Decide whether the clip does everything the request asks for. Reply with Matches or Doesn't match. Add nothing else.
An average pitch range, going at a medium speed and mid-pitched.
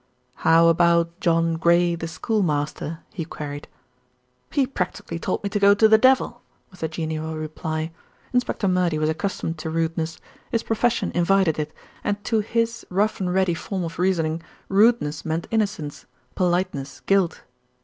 Matches